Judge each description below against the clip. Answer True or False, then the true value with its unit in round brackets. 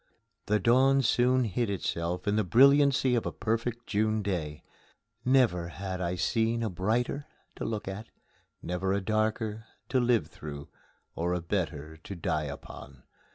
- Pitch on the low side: True (105 Hz)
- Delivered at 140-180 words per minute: True (155 wpm)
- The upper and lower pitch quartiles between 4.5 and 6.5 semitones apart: True (5.0 semitones)